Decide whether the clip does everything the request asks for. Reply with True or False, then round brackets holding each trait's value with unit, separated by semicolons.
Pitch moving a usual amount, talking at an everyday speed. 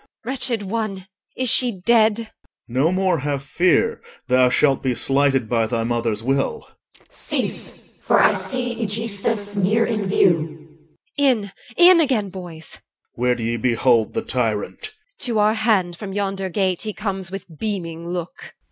False (8.3 semitones; 165 wpm)